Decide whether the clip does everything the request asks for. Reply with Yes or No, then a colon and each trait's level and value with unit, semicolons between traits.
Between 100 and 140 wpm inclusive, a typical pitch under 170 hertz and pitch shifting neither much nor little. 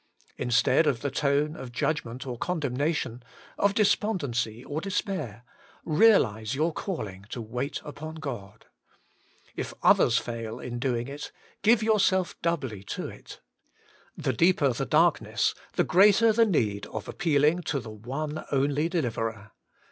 No: slow, 135 wpm; medium, 140 Hz; wide, 6.1 semitones